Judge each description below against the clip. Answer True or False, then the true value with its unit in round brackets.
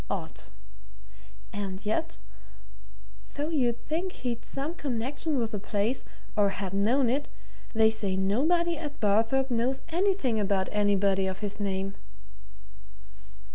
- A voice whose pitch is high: True (225 Hz)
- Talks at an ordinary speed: False (125 wpm)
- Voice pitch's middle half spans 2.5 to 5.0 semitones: False (5.6 semitones)